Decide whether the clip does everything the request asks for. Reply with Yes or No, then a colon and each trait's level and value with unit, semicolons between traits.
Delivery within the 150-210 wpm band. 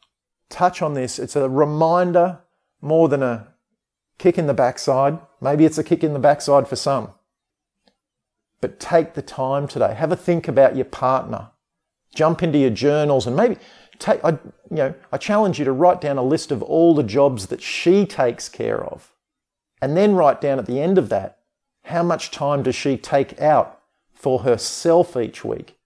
Yes: average, 185 wpm